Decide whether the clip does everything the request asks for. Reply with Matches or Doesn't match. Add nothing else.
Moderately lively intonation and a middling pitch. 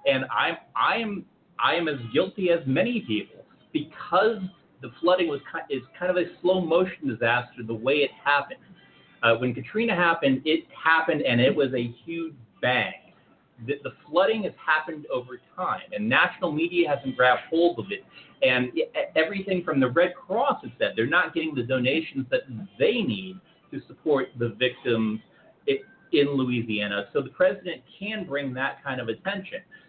Doesn't match